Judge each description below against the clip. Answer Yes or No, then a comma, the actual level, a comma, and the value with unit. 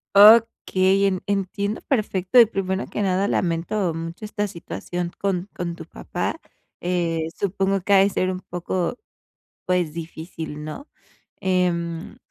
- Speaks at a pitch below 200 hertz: Yes, medium, 185 Hz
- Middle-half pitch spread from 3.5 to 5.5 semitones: No, average, 2.7 semitones